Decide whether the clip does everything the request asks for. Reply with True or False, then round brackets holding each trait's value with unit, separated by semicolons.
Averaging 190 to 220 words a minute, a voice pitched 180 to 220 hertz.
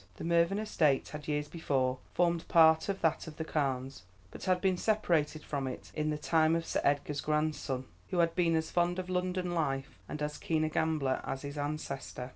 False (205 wpm; 155 Hz)